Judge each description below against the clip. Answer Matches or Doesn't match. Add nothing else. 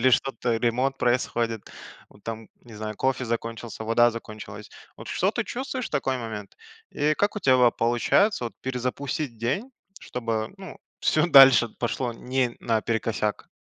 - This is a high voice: Doesn't match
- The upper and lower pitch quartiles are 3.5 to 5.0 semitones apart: Doesn't match